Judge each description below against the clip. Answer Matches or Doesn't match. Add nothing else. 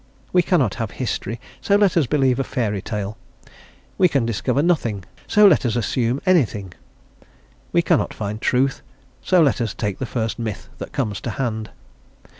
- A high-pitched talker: Doesn't match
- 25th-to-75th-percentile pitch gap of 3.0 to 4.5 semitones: Doesn't match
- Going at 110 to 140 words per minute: Doesn't match